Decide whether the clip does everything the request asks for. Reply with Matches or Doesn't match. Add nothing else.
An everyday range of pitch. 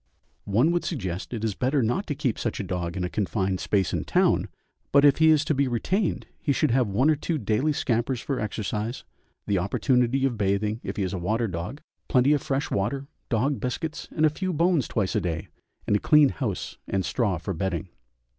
Doesn't match